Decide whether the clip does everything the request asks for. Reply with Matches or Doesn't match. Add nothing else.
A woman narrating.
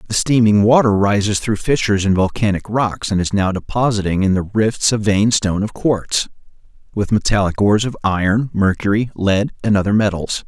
Doesn't match